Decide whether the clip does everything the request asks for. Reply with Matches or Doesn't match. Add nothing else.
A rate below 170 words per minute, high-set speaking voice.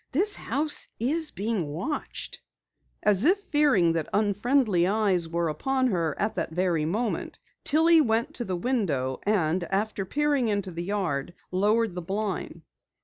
Matches